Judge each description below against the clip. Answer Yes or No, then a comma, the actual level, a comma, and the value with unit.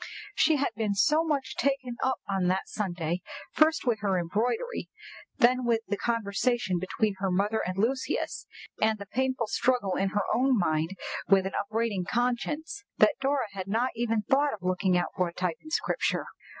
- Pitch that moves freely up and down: No, average, 4.9 semitones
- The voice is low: No, high, 220 Hz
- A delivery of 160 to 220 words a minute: Yes, average, 175 wpm